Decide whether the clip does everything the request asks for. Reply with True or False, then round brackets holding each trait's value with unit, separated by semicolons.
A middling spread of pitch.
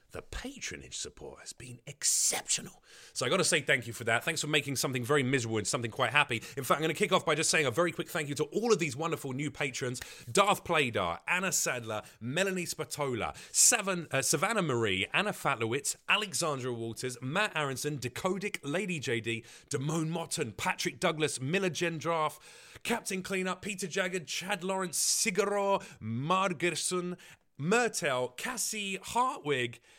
False (5.7 semitones)